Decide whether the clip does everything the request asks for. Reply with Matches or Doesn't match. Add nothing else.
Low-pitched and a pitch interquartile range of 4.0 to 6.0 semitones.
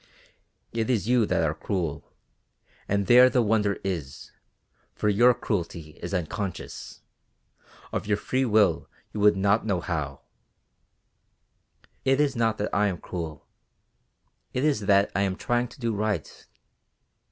Matches